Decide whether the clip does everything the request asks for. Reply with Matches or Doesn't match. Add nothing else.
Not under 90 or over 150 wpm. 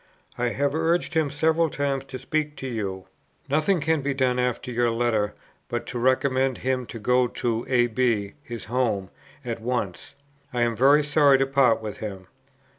Doesn't match